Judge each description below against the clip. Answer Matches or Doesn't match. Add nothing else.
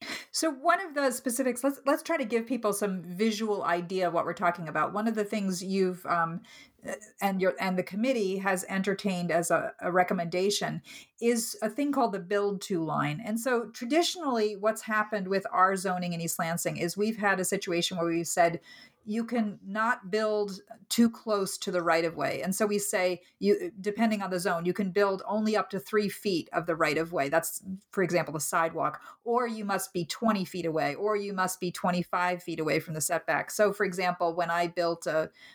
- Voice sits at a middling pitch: Doesn't match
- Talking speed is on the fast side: Matches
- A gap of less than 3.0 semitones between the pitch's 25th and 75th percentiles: Doesn't match